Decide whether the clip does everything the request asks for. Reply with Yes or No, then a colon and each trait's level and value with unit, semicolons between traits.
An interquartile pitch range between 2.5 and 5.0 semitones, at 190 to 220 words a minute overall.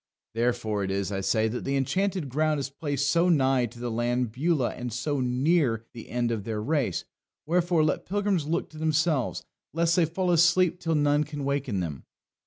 No: wide, 5.4 semitones; average, 195 wpm